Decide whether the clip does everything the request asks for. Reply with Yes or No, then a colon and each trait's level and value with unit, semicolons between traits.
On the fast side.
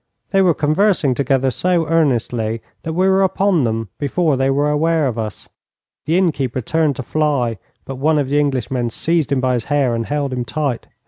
No: average, 195 wpm